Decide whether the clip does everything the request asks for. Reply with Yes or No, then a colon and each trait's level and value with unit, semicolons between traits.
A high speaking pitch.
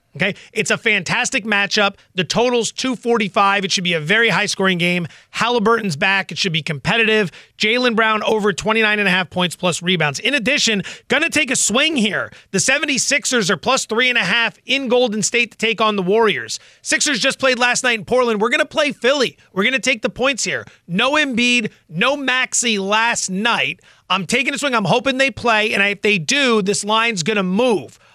Yes: high, 220 Hz